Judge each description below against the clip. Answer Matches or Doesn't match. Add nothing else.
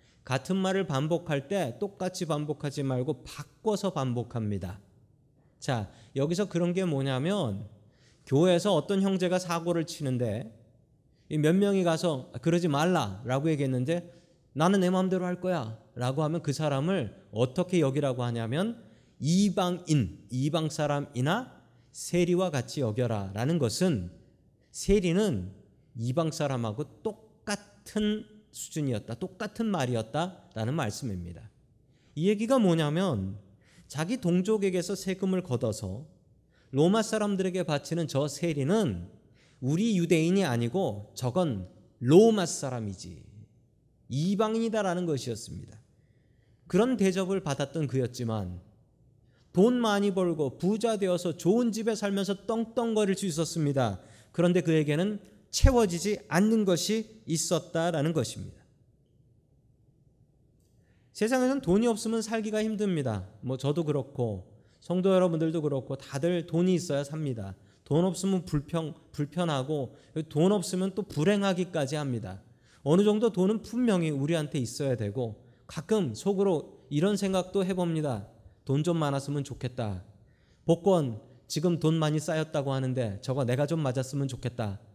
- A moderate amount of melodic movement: Doesn't match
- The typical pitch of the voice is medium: Matches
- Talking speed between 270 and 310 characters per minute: Matches